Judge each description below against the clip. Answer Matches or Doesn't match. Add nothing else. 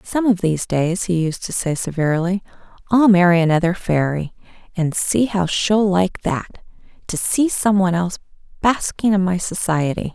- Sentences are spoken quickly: Doesn't match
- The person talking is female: Matches